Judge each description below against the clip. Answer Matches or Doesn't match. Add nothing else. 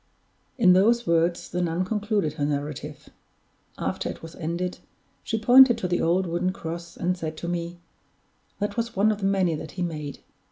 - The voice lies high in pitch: Doesn't match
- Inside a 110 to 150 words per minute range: Doesn't match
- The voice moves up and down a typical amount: Matches